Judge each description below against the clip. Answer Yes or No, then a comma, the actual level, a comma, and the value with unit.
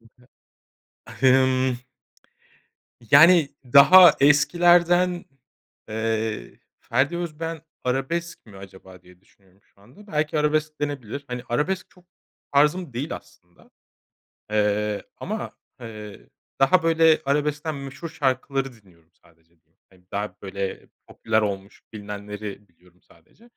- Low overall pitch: Yes, low, 130 Hz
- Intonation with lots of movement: Yes, wide, 7.0 semitones